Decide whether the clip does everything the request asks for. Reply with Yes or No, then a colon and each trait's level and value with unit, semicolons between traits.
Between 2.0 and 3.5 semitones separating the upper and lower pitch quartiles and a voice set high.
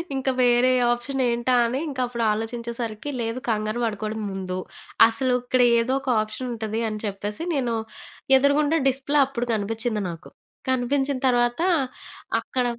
Yes: average, 2.9 semitones; high, 240 Hz